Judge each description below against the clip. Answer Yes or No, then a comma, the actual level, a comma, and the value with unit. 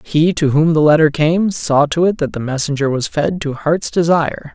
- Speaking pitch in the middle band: Yes, medium, 155 Hz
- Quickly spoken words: Yes, fast, 225 wpm